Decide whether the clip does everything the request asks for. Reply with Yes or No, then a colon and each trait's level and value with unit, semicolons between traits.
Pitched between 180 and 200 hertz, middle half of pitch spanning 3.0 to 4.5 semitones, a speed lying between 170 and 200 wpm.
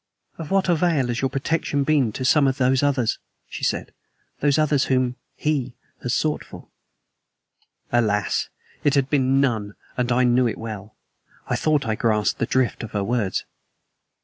No: low, 130 Hz; average, 3.5 semitones; average, 175 wpm